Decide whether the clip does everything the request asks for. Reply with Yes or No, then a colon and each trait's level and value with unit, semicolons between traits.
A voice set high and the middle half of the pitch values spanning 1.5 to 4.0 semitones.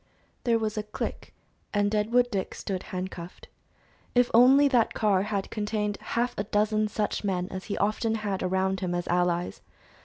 Yes: high, 210 Hz; average, 2.8 semitones